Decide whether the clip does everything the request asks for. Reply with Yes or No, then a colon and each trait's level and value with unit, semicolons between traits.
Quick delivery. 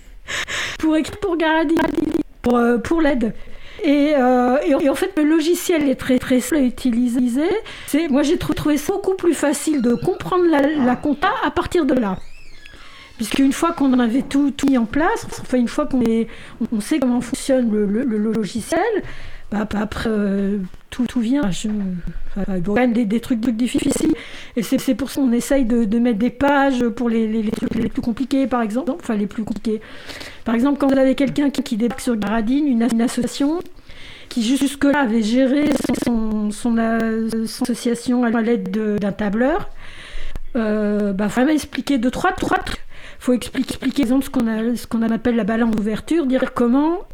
No: average, 195 wpm